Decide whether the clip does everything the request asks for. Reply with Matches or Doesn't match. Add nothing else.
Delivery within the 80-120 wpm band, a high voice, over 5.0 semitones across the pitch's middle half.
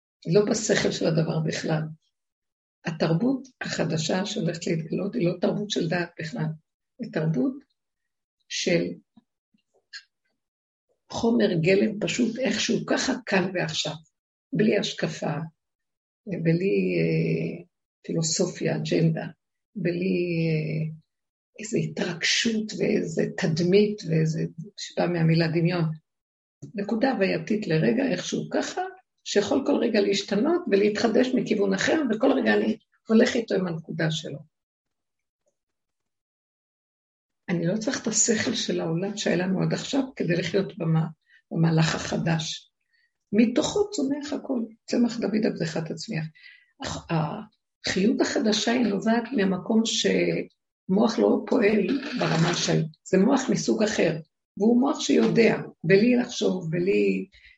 Matches